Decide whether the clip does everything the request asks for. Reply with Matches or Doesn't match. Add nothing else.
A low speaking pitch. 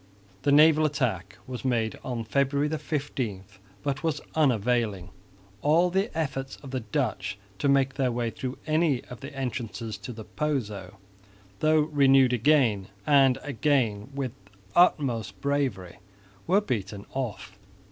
Matches